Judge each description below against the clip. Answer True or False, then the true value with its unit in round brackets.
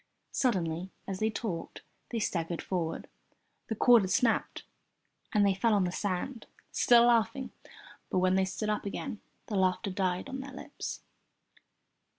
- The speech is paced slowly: False (155 wpm)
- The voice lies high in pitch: True (205 Hz)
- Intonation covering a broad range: False (4.0 semitones)